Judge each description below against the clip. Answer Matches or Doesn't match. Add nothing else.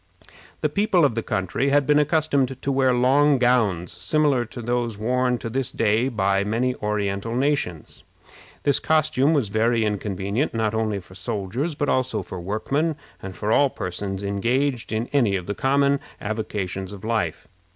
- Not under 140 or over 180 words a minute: Matches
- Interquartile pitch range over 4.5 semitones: Matches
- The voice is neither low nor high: Doesn't match